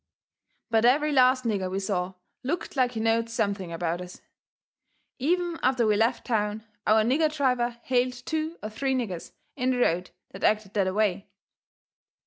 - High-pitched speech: Yes, high, 230 Hz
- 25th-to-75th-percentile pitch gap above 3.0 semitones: Yes, average, 4.2 semitones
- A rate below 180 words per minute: Yes, average, 160 wpm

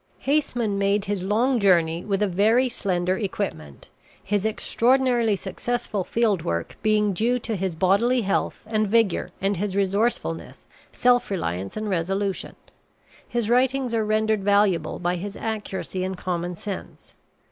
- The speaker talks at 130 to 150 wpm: Yes, average, 140 wpm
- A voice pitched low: No, high, 205 Hz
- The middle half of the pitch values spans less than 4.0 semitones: Yes, average, 3.4 semitones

